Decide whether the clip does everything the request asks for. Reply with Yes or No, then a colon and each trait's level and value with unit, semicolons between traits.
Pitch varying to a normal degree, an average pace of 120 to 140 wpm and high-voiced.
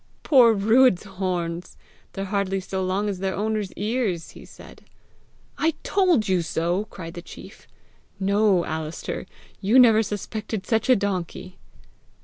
Yes: average, 3.1 semitones; slow, 135 wpm; high, 195 Hz